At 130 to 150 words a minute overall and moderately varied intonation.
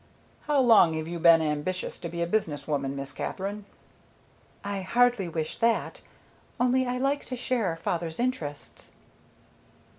No: average, 145 wpm; wide, 7.2 semitones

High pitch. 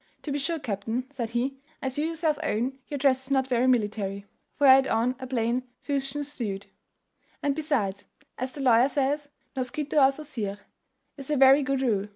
Yes: very high, 265 Hz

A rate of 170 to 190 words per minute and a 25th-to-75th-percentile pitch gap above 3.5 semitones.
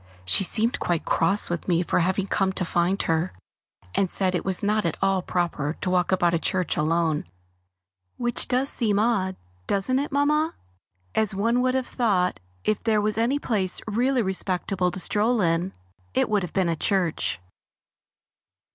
Yes: average, 175 wpm; average, 4.0 semitones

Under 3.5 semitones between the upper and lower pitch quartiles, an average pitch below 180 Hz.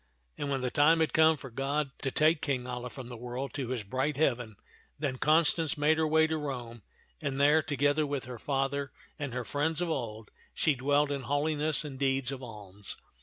Yes: average, 3.1 semitones; medium, 140 Hz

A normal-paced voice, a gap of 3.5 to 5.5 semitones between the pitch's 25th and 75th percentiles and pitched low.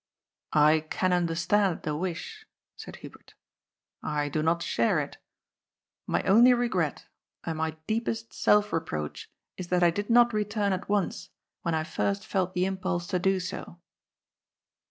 No: average, 155 wpm; average, 4.0 semitones; medium, 185 Hz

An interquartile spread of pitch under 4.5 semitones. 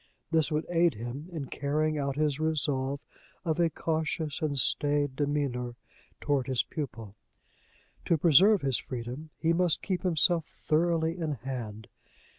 Yes: average, 3.3 semitones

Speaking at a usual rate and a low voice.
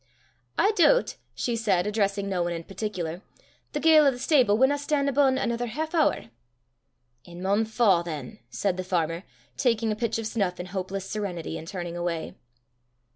No: average, 175 wpm; high, 205 Hz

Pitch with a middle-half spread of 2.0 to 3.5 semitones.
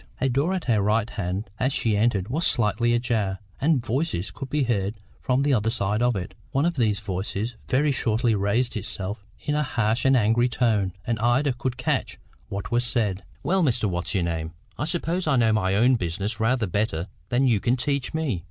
No: average, 4.2 semitones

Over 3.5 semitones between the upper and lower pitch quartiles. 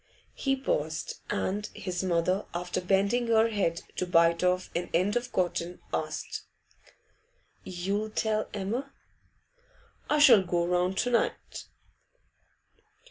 Yes: average, 4.0 semitones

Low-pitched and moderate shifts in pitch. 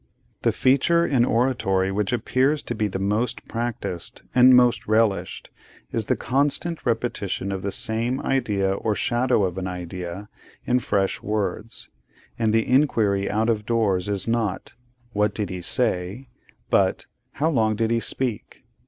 Yes: low, 110 Hz; average, 3.9 semitones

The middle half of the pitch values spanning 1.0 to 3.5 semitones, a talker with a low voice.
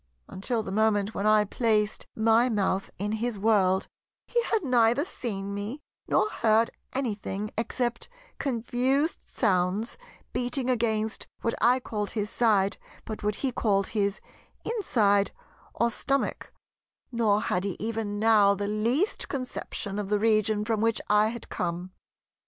No: average, 2.7 semitones; high, 220 Hz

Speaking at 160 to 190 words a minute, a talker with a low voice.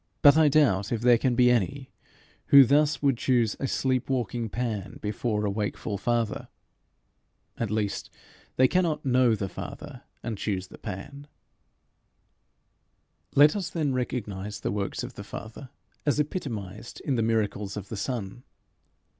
No: average, 150 wpm; low, 120 Hz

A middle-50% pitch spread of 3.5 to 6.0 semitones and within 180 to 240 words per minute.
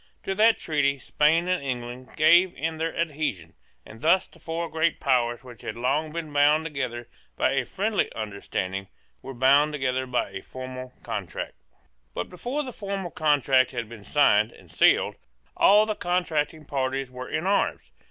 No: average, 4.8 semitones; average, 165 wpm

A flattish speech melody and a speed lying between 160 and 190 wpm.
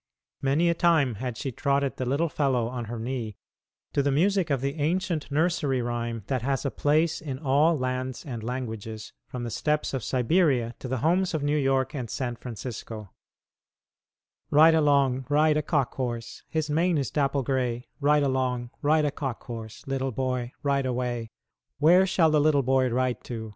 No: average, 3.5 semitones; average, 180 wpm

